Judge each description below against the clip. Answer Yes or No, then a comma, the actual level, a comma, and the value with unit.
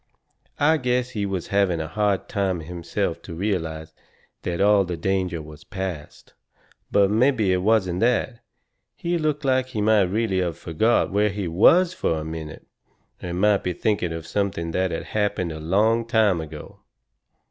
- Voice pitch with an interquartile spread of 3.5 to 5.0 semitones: Yes, average, 4.4 semitones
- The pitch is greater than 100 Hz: No, very low, 95 Hz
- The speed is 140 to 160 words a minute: No, average, 170 wpm